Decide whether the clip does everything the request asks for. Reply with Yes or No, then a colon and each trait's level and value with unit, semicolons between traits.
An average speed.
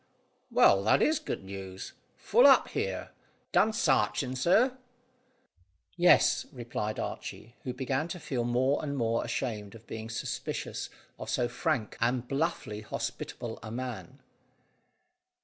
No: slow, 130 wpm